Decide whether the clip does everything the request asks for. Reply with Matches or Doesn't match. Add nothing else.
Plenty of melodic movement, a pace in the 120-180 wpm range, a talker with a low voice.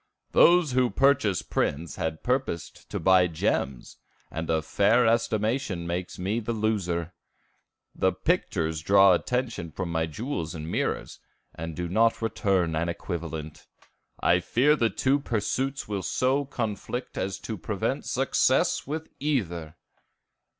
Matches